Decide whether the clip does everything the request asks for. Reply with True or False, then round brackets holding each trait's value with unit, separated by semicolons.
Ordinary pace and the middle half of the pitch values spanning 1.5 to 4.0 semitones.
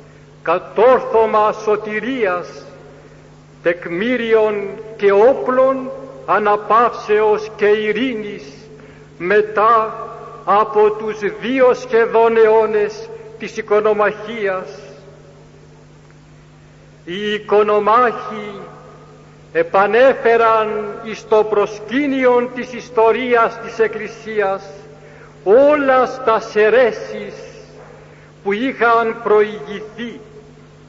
False (60 wpm; 2.4 semitones)